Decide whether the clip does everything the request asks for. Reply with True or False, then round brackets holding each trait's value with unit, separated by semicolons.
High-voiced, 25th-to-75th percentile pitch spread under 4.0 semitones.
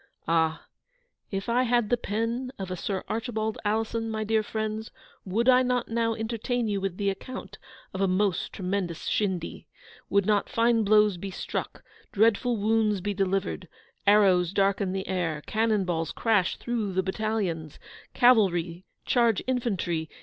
True (210 Hz; 3.2 semitones)